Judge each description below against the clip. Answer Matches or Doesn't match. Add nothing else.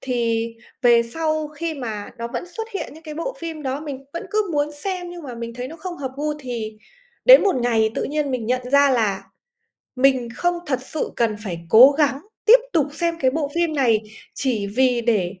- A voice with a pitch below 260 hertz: Doesn't match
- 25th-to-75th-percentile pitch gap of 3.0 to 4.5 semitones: Doesn't match